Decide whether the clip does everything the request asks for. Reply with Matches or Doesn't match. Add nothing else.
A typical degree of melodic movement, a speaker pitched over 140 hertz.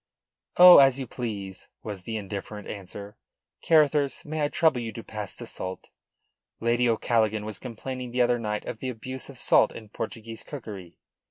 Doesn't match